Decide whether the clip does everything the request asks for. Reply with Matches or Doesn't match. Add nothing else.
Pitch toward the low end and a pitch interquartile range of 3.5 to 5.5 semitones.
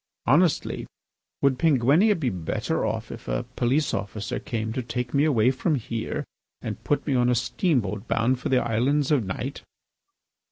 Matches